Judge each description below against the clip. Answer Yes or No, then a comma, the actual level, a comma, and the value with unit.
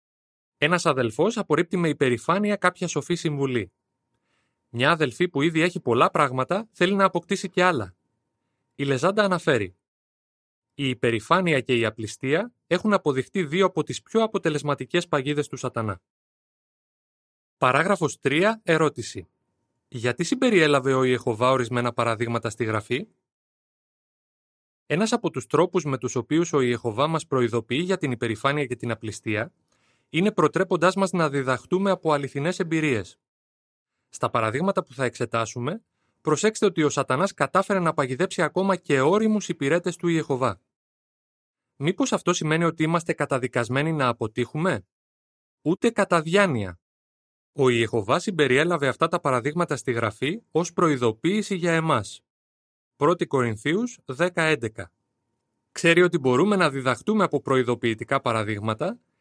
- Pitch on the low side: No, medium, 145 Hz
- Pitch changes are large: Yes, wide, 6.5 semitones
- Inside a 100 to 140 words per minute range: Yes, average, 130 wpm